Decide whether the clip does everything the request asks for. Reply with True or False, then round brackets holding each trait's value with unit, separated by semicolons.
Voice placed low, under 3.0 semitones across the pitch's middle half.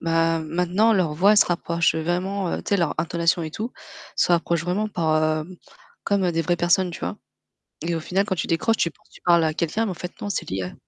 False (170 Hz; 2.4 semitones)